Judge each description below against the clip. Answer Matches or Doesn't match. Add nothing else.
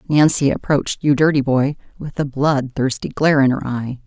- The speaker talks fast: Doesn't match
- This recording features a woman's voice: Matches